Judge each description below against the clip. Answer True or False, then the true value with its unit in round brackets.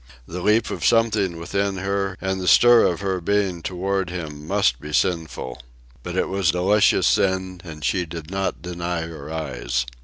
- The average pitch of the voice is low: True (90 Hz)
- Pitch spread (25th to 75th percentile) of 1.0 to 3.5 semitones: True (3.0 semitones)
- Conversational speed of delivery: True (175 wpm)